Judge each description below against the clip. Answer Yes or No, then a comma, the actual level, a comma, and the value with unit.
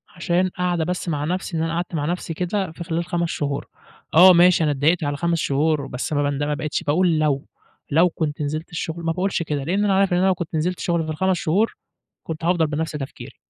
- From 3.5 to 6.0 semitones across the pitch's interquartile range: No, average, 2.8 semitones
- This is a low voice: No, medium, 165 Hz